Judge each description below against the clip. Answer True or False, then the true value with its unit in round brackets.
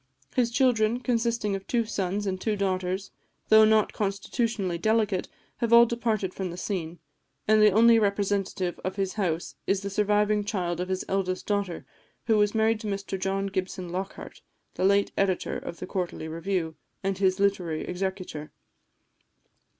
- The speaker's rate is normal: True (160 wpm)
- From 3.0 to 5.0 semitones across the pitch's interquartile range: False (2.6 semitones)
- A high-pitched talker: True (195 Hz)